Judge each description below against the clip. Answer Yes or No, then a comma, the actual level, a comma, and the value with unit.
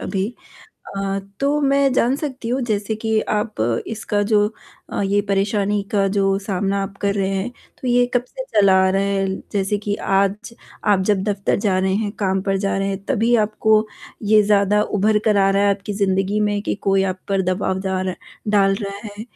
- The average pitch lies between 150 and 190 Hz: No, high, 200 Hz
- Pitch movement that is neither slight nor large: No, narrow, 1.6 semitones